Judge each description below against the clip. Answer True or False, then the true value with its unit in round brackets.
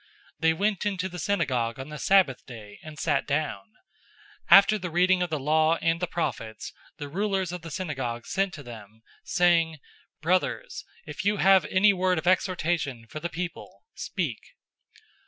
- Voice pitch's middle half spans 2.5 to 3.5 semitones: False (4.5 semitones)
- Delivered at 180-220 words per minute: False (170 wpm)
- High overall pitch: False (165 Hz)